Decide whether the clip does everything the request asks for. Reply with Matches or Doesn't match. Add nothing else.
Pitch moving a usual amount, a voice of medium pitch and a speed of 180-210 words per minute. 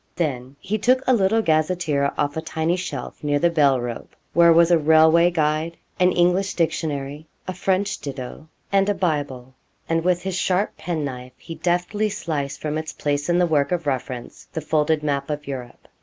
Matches